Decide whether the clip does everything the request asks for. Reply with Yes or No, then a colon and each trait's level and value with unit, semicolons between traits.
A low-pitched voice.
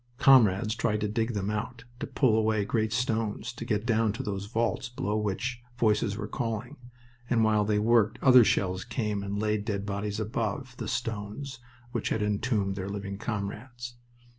Yes: low, 110 Hz